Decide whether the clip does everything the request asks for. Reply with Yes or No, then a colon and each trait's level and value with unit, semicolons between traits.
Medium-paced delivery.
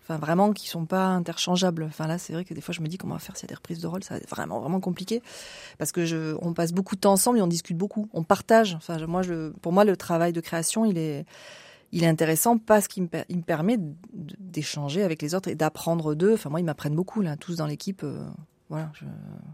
No: fast, 260 wpm